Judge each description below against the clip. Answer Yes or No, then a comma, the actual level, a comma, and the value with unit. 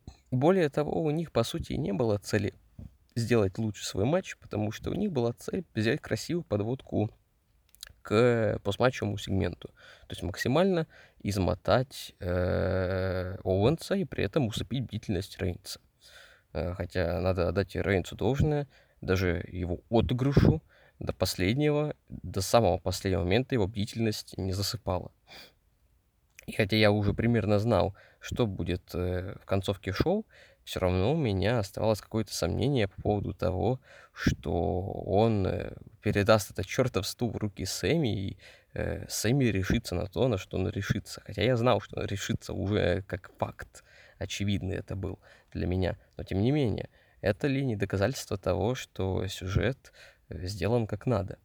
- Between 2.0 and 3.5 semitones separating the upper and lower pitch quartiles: No, average, 4.2 semitones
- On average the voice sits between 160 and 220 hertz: No, low, 105 Hz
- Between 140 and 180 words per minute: Yes, average, 145 wpm